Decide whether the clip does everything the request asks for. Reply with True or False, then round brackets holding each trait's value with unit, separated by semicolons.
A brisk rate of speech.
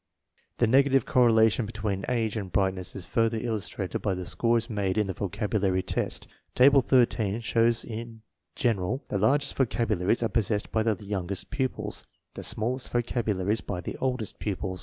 False (165 wpm)